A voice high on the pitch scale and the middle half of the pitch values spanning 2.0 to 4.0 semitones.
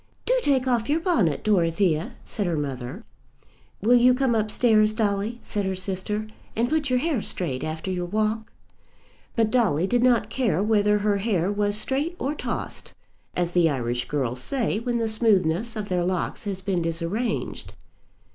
No: high, 210 Hz; average, 5.0 semitones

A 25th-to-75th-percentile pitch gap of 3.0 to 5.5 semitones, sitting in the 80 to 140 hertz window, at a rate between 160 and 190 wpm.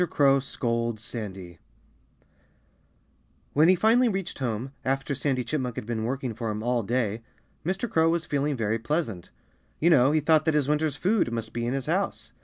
Yes: average, 5.1 semitones; low, 135 Hz; average, 180 wpm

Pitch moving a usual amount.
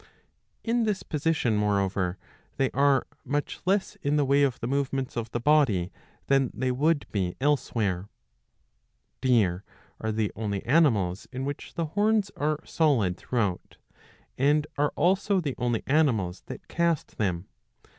No: wide, 6.3 semitones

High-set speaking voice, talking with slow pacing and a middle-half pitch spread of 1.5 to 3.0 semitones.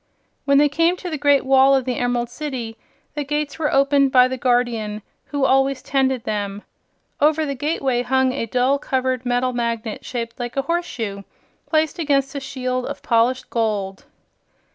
No: very high, 260 Hz; average, 175 wpm; narrow, 2.6 semitones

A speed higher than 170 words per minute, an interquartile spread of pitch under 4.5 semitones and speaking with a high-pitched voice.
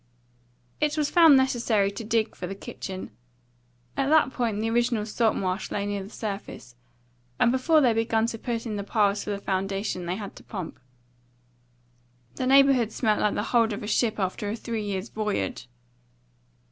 Yes: average, 180 wpm; average, 3.0 semitones; high, 220 Hz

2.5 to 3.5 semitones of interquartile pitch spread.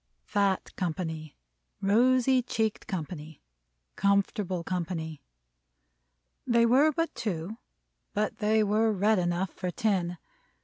No: average, 4.1 semitones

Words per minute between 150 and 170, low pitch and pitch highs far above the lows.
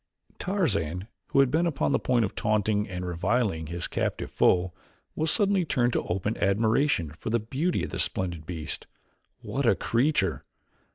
Yes: average, 165 wpm; low, 105 Hz; wide, 7.6 semitones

